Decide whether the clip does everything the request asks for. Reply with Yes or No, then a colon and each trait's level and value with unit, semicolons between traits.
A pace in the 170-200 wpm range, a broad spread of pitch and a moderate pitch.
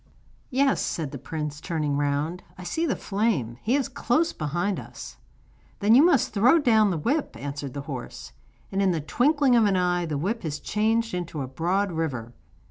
Yes: average, 190 wpm; wide, 7.6 semitones; medium, 180 Hz